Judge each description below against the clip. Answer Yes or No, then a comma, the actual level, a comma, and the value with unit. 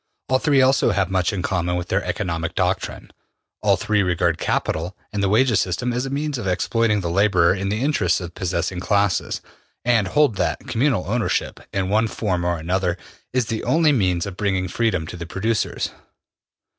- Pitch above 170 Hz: No, low, 100 Hz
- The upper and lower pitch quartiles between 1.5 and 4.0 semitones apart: No, average, 4.4 semitones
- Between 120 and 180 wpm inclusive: No, average, 190 wpm